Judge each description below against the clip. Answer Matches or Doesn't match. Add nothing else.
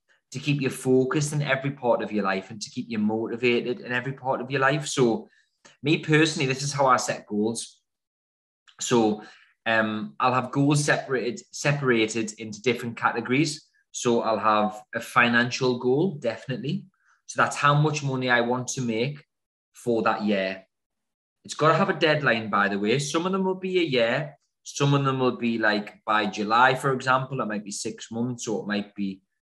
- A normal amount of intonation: Matches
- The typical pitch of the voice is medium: Doesn't match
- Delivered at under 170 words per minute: Doesn't match